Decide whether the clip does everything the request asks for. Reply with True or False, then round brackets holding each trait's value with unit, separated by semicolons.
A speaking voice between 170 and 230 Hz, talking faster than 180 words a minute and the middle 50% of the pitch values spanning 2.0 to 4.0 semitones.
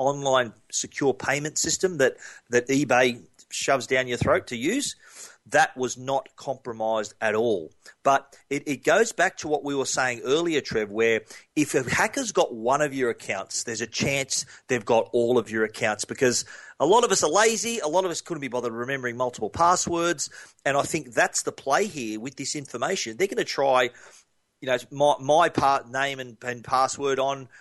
False (135 Hz; 195 wpm; 3.4 semitones)